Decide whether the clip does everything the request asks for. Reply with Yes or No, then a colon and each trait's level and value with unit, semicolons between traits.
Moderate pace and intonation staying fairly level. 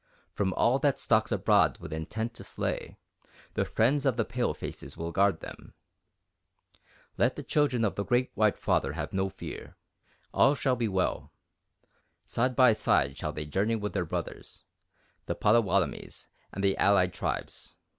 No: average, 155 wpm; average, 4.7 semitones